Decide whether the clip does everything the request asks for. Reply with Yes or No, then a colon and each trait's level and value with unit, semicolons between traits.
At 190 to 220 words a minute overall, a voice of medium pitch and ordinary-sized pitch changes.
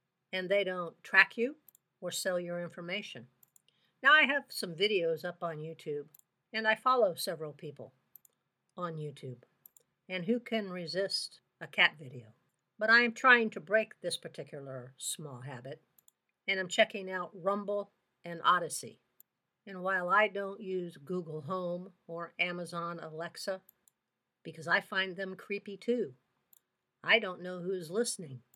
No: average, 145 wpm; medium, 180 Hz; average, 3.5 semitones